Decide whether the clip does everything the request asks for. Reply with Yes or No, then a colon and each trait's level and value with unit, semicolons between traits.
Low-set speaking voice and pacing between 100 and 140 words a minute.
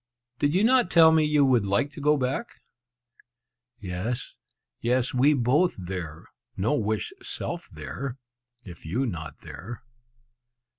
Yes: low, 125 Hz; slow, 135 wpm